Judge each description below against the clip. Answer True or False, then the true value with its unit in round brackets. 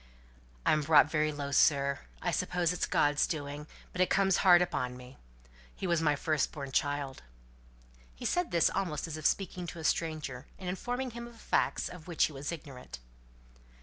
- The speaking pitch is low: False (155 Hz)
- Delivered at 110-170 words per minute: False (180 wpm)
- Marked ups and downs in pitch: False (3.8 semitones)